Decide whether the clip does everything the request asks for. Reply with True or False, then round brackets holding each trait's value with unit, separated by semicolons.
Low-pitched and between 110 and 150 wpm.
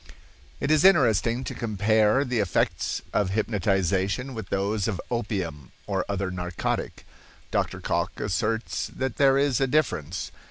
True (110 Hz; 135 wpm)